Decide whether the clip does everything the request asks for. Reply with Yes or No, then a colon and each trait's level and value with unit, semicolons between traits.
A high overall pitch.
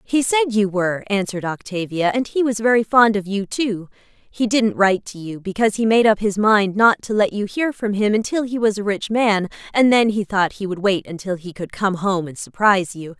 Yes: high, 205 Hz